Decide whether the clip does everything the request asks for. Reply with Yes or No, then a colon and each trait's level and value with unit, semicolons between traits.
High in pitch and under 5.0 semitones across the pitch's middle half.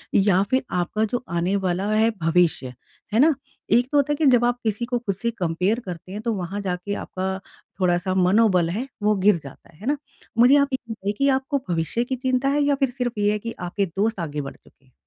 No: high, 205 Hz; wide, 5.4 semitones